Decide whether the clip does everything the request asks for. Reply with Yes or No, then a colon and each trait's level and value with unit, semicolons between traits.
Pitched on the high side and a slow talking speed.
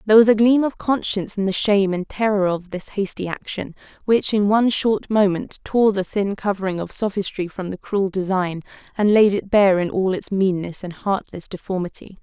No: high, 200 Hz; average, 200 wpm